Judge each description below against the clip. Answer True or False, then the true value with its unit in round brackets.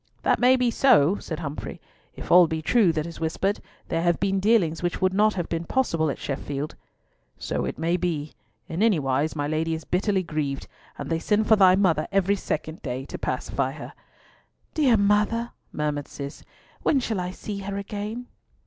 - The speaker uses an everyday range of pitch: True (4.7 semitones)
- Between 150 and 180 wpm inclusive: False (190 wpm)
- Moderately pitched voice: True (180 Hz)